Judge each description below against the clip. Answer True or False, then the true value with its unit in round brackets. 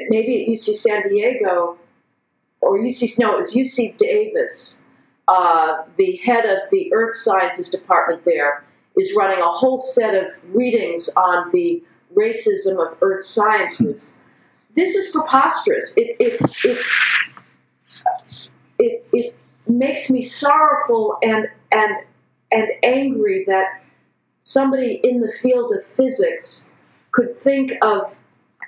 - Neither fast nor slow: False (125 wpm)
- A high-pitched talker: True (250 Hz)